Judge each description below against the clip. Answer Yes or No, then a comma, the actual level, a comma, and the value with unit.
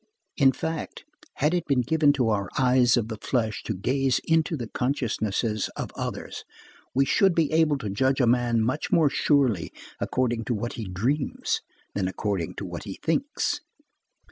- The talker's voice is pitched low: Yes, low, 125 Hz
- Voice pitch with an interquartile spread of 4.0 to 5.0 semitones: Yes, average, 4.7 semitones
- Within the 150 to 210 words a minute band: Yes, average, 170 wpm